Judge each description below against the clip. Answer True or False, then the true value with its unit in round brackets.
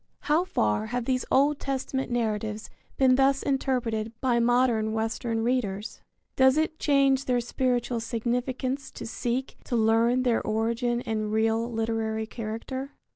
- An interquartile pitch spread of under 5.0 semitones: True (2.8 semitones)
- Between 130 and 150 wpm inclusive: True (135 wpm)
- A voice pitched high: True (240 Hz)